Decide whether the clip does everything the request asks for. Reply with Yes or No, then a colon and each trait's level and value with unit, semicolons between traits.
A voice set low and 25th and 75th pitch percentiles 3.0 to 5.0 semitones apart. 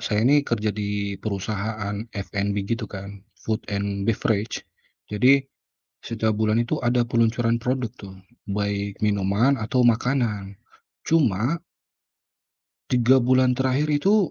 Yes: low, 110 Hz; average, 3.7 semitones